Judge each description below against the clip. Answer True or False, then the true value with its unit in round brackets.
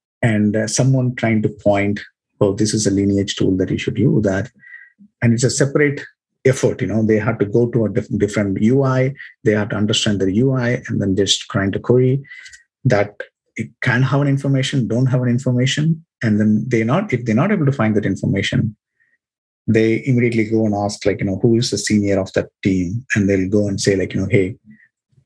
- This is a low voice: True (115 Hz)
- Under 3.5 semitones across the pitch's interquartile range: False (4.0 semitones)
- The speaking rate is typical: False (215 wpm)